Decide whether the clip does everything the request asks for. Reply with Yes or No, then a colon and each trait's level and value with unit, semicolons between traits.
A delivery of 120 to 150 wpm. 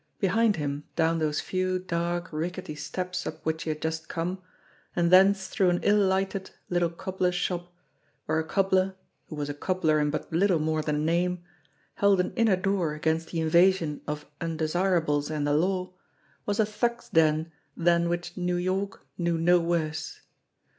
No: average, 170 wpm